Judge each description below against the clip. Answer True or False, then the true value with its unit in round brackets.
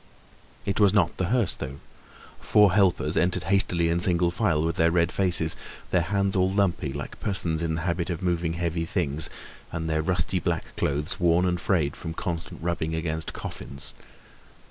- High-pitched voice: False (85 Hz)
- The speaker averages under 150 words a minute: False (175 wpm)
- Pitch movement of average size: False (2.3 semitones)